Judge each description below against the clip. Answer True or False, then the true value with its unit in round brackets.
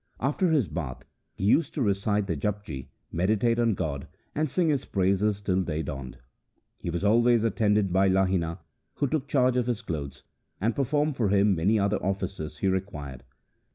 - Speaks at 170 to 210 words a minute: True (175 wpm)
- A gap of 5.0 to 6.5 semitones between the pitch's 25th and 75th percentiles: True (5.3 semitones)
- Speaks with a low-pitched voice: True (100 Hz)